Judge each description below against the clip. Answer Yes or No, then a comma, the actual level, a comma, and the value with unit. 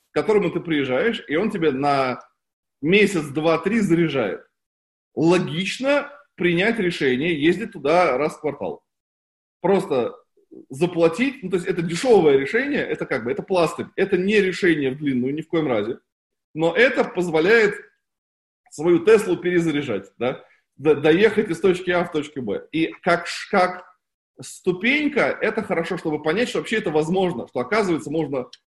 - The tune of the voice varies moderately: Yes, average, 4.9 semitones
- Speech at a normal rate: Yes, average, 150 wpm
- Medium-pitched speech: Yes, medium, 175 Hz